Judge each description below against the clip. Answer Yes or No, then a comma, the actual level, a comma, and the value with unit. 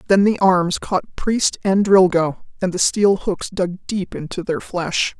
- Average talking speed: Yes, average, 185 wpm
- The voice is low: No, medium, 185 Hz